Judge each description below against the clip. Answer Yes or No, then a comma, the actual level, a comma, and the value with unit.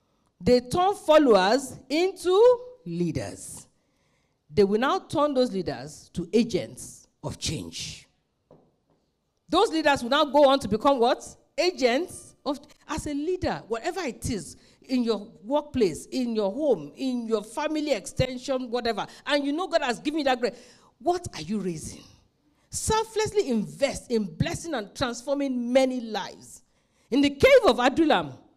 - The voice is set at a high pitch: Yes, very high, 265 Hz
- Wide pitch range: Yes, wide, 5.7 semitones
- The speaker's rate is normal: Yes, average, 145 wpm